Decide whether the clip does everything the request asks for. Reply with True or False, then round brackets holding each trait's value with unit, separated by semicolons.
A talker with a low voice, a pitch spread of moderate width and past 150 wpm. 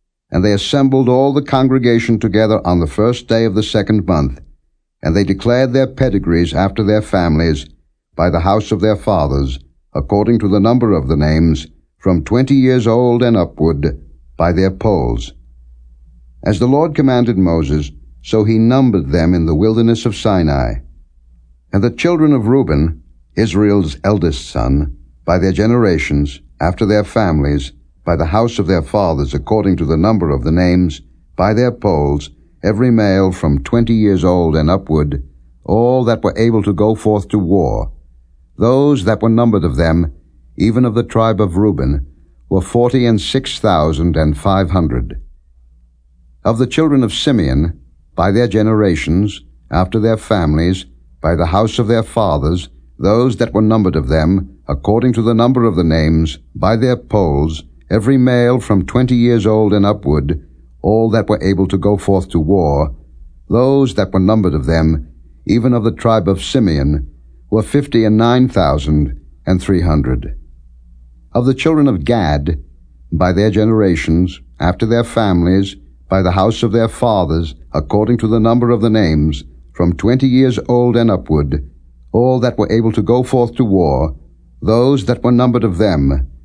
False (95 Hz; 7.4 semitones; 165 wpm)